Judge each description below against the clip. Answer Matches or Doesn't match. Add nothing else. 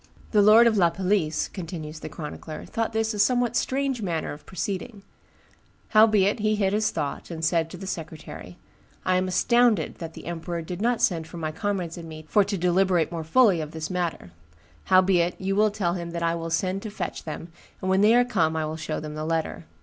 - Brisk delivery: Matches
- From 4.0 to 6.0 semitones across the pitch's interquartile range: Matches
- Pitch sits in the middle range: Matches